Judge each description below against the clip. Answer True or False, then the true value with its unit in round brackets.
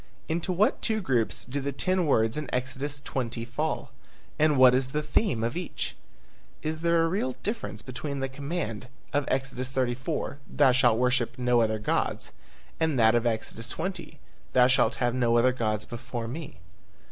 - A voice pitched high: False (130 Hz)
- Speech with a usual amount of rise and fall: True (4.0 semitones)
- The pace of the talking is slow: False (170 wpm)